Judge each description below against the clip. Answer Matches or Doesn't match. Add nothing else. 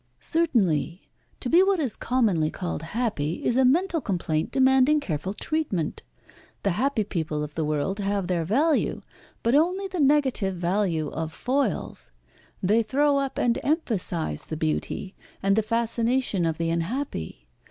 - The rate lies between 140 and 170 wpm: Matches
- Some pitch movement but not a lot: Doesn't match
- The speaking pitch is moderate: Doesn't match